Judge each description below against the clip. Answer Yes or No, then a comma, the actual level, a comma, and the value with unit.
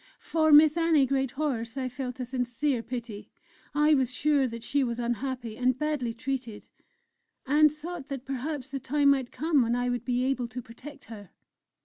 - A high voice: Yes, very high, 260 Hz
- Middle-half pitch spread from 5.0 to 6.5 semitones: No, average, 3.2 semitones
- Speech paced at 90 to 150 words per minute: No, average, 175 wpm